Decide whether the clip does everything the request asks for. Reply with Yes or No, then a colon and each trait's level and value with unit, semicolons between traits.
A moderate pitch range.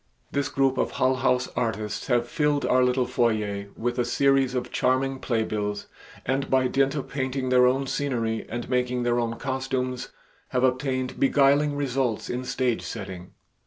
No: narrow, 1.9 semitones